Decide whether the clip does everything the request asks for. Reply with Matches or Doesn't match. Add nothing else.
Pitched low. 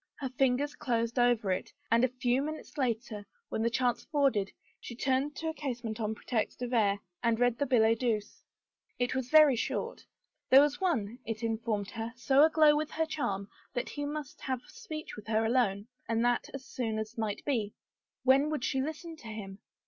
Doesn't match